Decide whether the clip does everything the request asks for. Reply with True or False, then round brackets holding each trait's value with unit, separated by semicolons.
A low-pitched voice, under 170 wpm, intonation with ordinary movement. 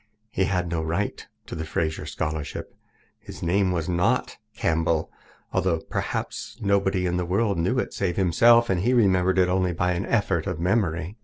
False (90 Hz; 175 wpm; 3.0 semitones)